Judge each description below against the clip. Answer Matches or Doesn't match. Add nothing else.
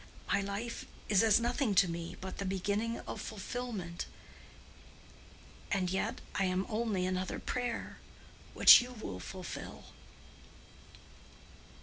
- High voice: Matches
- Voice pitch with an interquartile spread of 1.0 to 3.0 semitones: Doesn't match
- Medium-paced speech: Doesn't match